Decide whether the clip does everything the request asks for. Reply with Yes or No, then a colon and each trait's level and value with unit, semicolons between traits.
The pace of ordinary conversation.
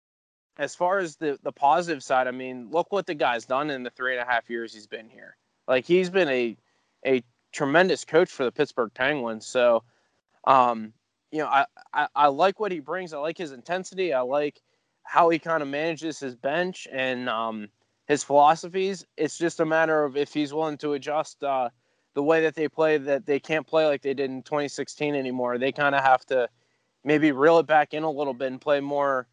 No: fast, 215 wpm